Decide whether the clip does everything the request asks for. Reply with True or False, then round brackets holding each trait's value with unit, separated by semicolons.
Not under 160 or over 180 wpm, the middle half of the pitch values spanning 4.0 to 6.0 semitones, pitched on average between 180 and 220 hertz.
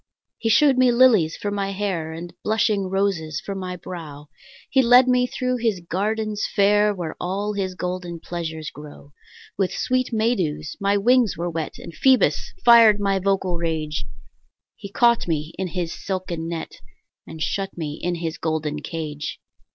True (165 wpm; 4.5 semitones; 185 Hz)